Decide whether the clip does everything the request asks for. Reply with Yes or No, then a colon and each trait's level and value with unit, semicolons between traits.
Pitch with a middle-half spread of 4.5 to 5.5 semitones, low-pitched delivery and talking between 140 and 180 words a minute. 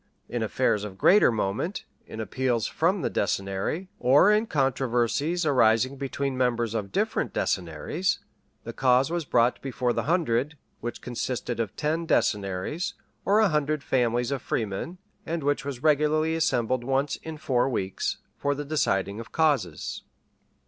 Yes: average, 5.0 semitones; low, 130 Hz; average, 150 wpm